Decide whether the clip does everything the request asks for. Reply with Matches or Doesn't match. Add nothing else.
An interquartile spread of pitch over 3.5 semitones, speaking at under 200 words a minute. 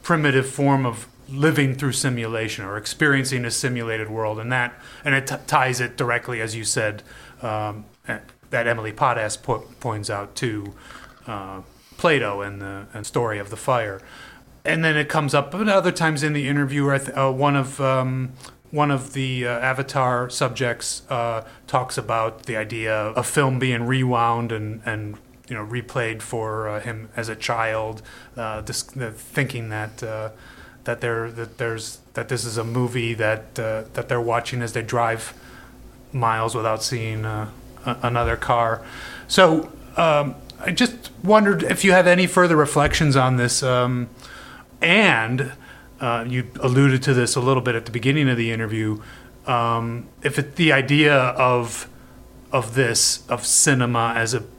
Doesn't match